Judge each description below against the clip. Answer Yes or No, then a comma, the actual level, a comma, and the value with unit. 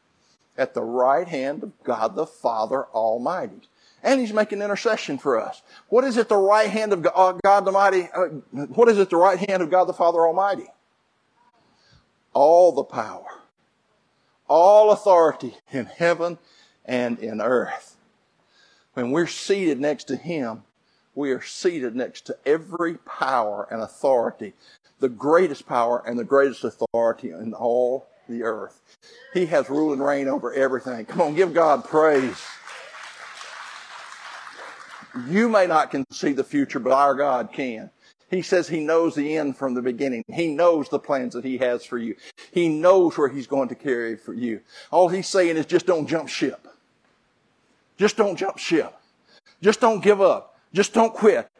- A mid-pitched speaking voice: Yes, medium, 170 Hz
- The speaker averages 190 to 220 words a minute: No, average, 165 wpm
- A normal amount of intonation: No, wide, 6.9 semitones